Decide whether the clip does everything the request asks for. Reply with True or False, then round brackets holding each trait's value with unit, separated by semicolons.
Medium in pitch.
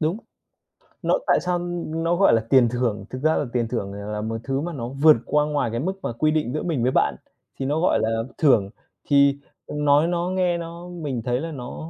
True (145 Hz)